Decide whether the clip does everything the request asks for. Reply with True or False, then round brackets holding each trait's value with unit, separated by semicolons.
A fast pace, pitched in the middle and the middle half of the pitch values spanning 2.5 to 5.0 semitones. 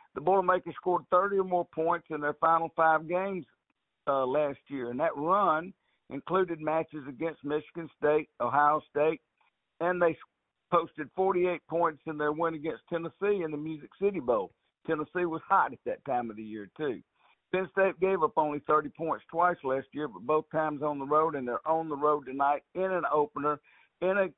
False (190 wpm; 160 Hz; 2.8 semitones)